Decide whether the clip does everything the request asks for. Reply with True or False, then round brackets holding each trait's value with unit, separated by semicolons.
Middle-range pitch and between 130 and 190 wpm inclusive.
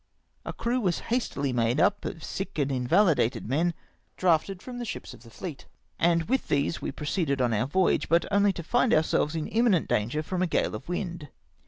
False (165 Hz; 200 wpm)